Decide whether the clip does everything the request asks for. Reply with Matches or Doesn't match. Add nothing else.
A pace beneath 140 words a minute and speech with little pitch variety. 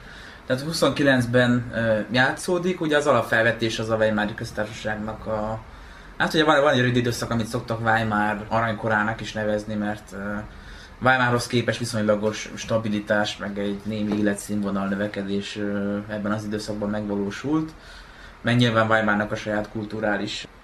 Matches